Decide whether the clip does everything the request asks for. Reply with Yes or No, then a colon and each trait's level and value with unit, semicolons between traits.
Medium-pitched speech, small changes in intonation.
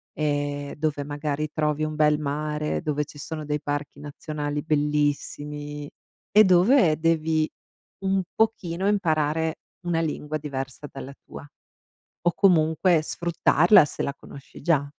Yes: medium, 150 Hz; narrow, 1.9 semitones